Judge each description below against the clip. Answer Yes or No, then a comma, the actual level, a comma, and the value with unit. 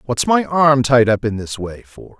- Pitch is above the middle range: No, low, 125 Hz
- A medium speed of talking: No, fast, 245 wpm